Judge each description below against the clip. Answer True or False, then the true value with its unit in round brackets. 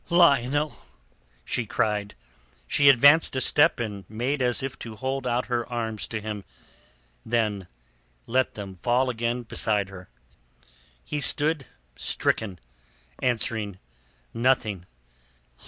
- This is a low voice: True (120 Hz)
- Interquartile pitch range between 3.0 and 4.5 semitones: True (3.8 semitones)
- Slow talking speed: True (115 wpm)